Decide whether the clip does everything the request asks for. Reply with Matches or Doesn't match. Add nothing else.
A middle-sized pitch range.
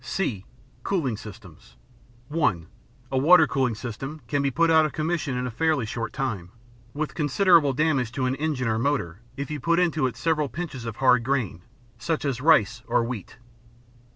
Matches